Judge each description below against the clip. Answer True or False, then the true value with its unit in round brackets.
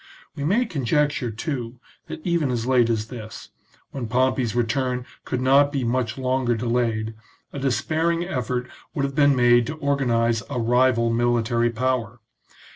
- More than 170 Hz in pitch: False (125 Hz)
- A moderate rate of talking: True (150 wpm)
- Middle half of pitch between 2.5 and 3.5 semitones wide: True (2.9 semitones)